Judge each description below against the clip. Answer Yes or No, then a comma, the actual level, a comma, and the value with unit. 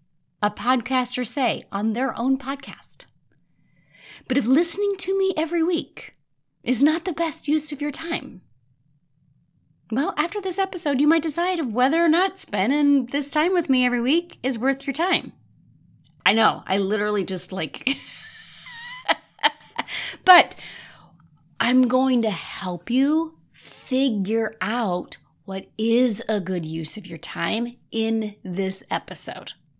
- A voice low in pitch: No, very high, 255 Hz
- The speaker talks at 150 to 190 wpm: No, average, 140 wpm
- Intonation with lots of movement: Yes, wide, 8.2 semitones